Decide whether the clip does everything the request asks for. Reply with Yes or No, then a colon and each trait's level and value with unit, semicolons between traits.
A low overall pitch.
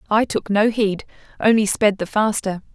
No: high, 210 Hz